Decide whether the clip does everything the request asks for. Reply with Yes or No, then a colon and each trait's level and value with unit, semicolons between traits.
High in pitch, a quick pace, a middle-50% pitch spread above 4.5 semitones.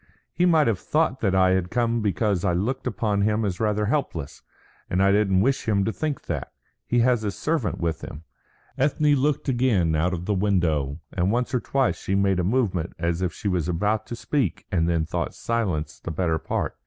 No: low, 100 Hz; fast, 210 wpm; wide, 5.4 semitones